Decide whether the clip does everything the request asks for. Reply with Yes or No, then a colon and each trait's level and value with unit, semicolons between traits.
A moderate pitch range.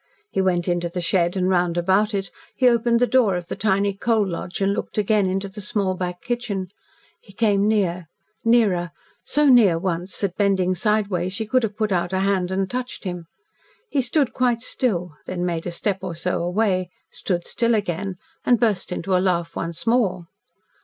Yes: average, 3.5 semitones